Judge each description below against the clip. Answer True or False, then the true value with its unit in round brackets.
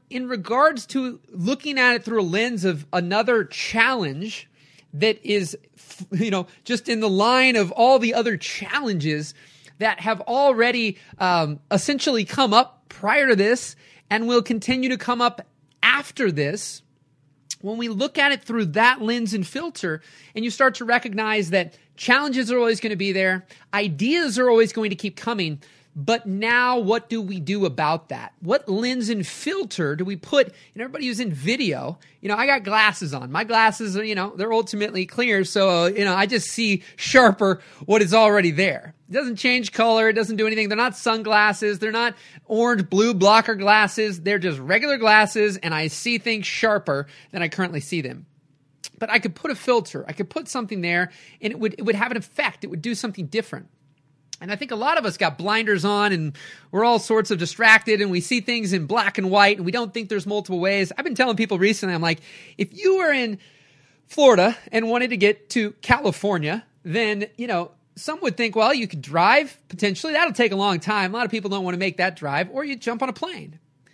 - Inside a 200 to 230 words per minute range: True (205 wpm)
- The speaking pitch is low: False (210 Hz)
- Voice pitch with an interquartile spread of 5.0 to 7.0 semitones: False (4.6 semitones)